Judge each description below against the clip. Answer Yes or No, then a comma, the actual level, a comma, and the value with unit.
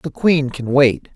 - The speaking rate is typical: No, fast, 210 wpm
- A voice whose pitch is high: No, medium, 140 Hz